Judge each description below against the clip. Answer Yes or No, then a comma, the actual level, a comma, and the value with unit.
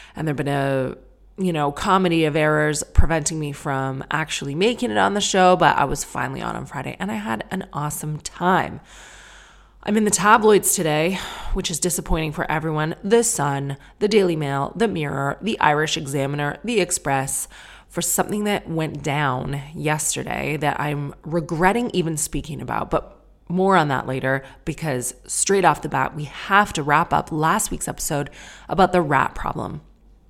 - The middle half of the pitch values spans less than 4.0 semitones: No, average, 4.5 semitones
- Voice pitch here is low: No, medium, 160 Hz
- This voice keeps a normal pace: Yes, average, 170 wpm